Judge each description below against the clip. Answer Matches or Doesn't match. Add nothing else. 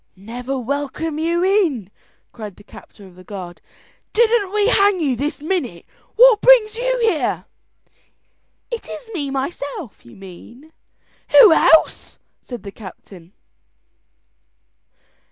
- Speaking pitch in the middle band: Doesn't match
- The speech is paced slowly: Matches